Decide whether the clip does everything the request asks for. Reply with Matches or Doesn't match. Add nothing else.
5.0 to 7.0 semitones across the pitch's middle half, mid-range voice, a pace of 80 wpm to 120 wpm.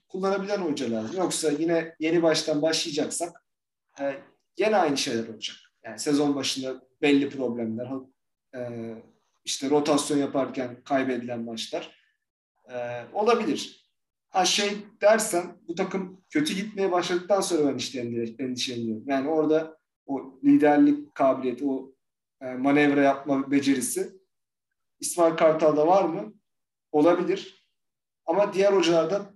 Matches